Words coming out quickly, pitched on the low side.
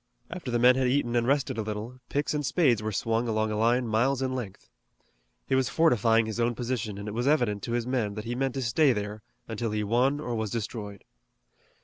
Yes: fast, 230 wpm; low, 120 Hz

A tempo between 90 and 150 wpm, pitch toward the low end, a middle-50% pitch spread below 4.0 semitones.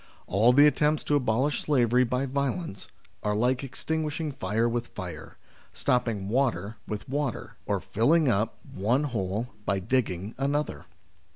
No: slow, 135 wpm; low, 125 Hz; average, 5.1 semitones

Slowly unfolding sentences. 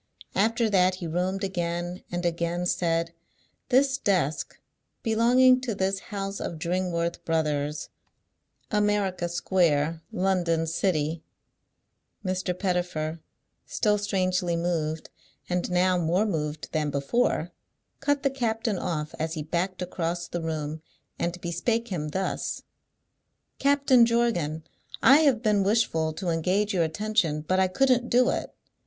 Yes: slow, 130 wpm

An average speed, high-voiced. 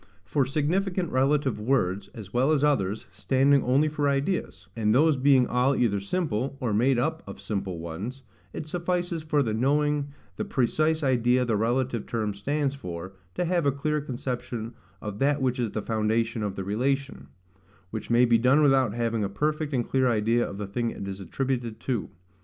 No: average, 185 wpm; low, 125 Hz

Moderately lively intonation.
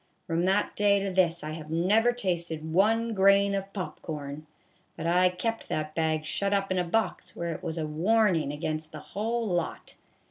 Yes: average, 4.1 semitones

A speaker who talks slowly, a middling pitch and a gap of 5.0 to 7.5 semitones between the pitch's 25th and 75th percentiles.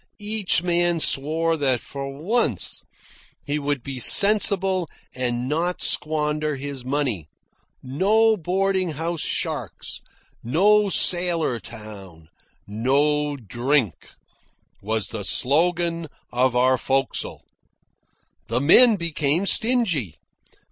Yes: slow, 100 wpm; medium, 150 Hz; wide, 5.6 semitones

